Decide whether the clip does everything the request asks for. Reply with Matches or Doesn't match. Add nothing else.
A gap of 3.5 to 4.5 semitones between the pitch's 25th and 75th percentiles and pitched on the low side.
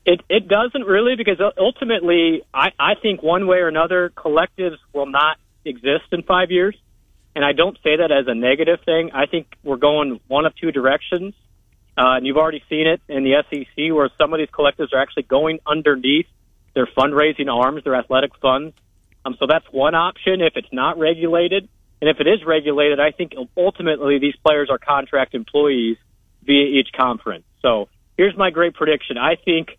Doesn't match